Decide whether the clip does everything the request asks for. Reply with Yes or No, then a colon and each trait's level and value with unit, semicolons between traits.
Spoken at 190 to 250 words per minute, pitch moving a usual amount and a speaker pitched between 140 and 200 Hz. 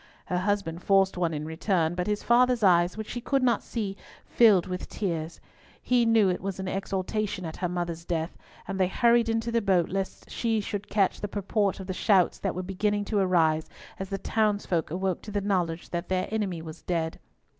Yes: fast, 205 wpm; average, 3.1 semitones; high, 190 Hz